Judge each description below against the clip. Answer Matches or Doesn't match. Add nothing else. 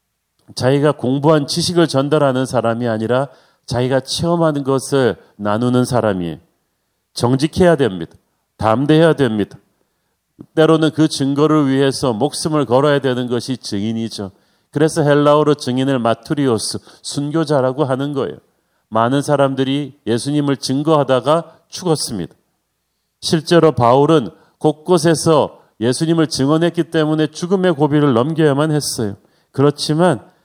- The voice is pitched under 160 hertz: Matches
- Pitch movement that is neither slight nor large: Matches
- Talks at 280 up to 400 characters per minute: Matches